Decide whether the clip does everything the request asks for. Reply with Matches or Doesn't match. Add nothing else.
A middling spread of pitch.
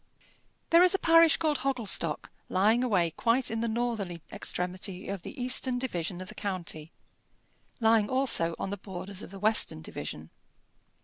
Doesn't match